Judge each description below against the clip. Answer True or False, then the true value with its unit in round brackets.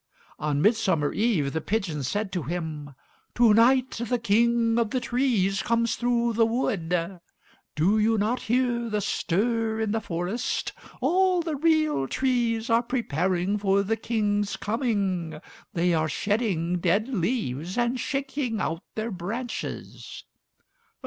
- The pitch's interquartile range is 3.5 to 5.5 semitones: True (5.0 semitones)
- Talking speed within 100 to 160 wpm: True (135 wpm)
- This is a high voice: True (220 Hz)